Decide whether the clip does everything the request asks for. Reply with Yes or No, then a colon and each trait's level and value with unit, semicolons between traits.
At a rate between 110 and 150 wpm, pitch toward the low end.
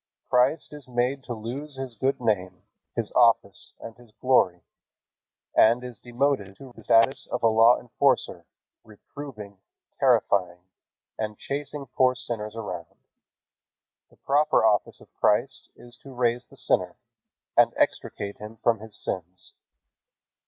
Yes: slow, 135 wpm; low, 120 Hz